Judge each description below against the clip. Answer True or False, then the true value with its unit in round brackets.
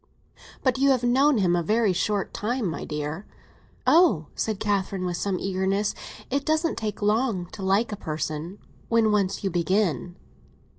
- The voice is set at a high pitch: True (200 Hz)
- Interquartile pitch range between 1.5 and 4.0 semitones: False (4.4 semitones)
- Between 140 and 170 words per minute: True (155 wpm)